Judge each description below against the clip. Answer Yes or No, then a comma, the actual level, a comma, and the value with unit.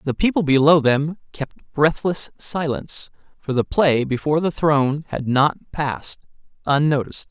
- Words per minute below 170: Yes, average, 140 wpm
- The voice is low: No, medium, 150 Hz